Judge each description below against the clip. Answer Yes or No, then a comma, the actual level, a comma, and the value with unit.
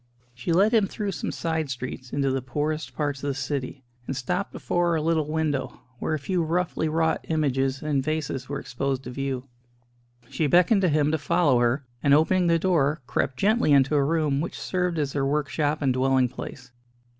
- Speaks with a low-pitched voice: No, medium, 150 Hz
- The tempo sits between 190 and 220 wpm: Yes, average, 195 wpm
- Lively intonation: No, average, 3.5 semitones